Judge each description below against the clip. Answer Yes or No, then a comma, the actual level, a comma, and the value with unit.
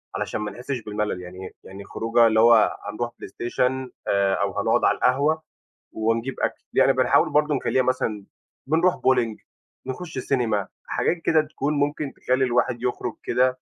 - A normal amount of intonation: Yes, average, 3.8 semitones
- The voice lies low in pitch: Yes, low, 125 Hz